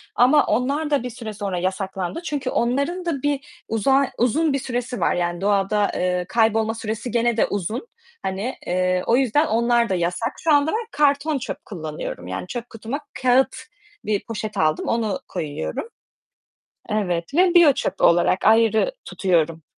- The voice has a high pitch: Yes, high, 230 Hz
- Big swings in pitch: Yes, wide, 6.3 semitones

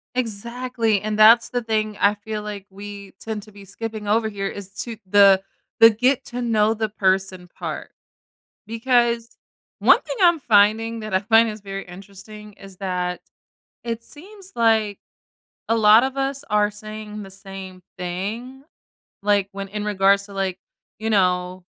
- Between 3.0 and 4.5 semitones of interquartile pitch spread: No, narrow, 2.5 semitones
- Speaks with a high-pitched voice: Yes, high, 210 Hz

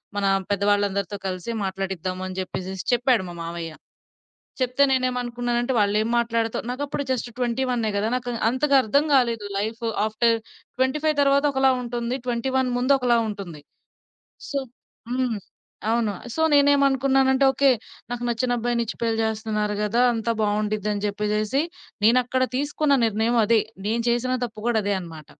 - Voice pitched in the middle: No, high, 235 Hz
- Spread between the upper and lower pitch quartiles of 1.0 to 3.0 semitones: No, average, 3.5 semitones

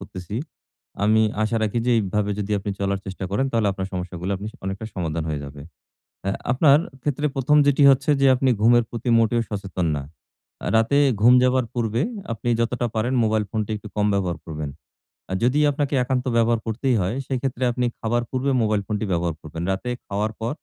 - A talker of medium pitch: No, low, 110 Hz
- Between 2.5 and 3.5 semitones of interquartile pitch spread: No, average, 4.2 semitones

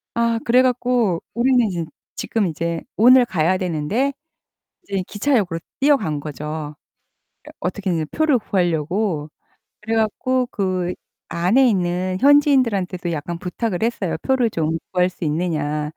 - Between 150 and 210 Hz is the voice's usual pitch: Yes, medium, 185 Hz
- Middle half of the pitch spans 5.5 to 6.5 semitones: Yes, wide, 6.0 semitones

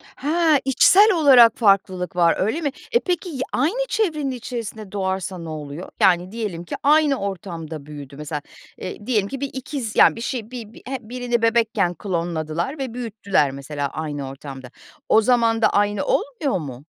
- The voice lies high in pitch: Yes, high, 215 Hz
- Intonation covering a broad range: Yes, wide, 7.4 semitones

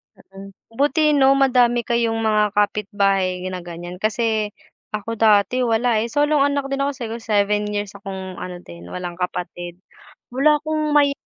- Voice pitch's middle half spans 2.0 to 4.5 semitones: No, wide, 5.6 semitones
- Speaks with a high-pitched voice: Yes, high, 220 Hz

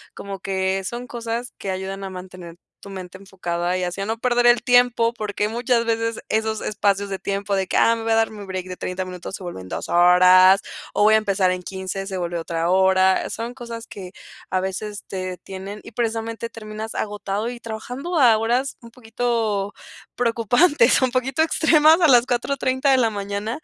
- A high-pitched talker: Yes, high, 215 Hz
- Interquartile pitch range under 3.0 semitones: No, average, 3.8 semitones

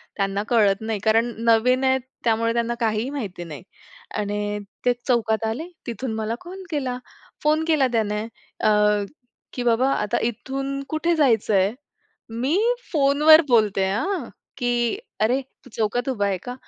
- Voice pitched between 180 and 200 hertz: No, high, 235 Hz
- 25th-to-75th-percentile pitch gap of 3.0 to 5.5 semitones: Yes, average, 3.7 semitones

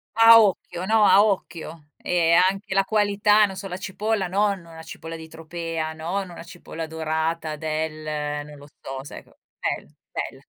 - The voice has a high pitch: No, medium, 170 Hz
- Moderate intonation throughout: Yes, average, 3.7 semitones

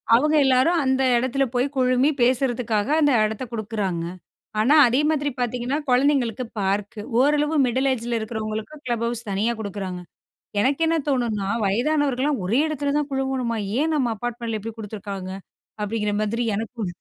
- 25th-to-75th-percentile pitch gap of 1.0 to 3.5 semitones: No, average, 3.9 semitones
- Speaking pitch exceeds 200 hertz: Yes, high, 240 Hz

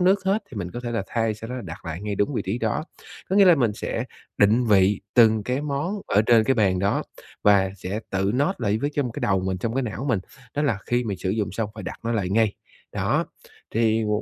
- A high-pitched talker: No, low, 110 Hz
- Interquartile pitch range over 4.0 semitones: No, average, 3.7 semitones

